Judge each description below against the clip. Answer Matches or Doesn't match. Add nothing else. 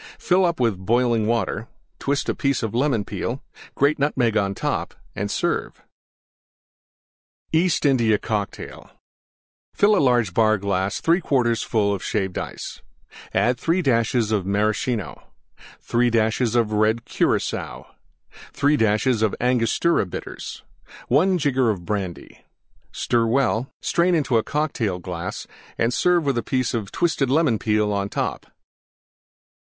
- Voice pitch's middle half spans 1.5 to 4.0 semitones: Doesn't match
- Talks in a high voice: Doesn't match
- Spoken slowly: Matches